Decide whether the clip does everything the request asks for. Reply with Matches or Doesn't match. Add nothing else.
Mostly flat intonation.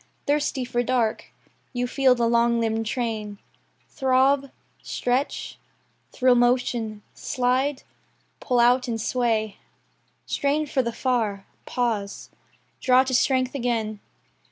Matches